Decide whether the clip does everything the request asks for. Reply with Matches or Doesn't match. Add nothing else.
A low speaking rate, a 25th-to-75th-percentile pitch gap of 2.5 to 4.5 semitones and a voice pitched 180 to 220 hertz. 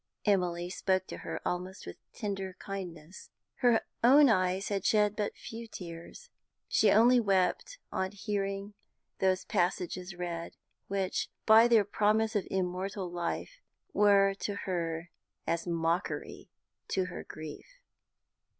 Matches